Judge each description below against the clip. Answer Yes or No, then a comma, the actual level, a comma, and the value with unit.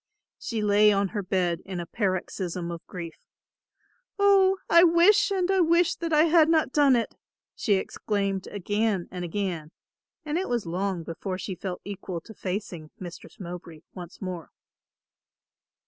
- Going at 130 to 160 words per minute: Yes, average, 155 wpm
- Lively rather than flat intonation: Yes, wide, 9.0 semitones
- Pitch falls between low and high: No, high, 200 Hz